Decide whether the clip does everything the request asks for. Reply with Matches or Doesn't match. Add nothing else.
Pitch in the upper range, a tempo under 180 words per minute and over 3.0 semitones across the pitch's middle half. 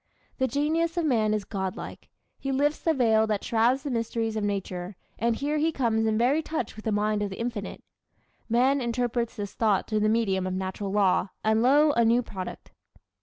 Doesn't match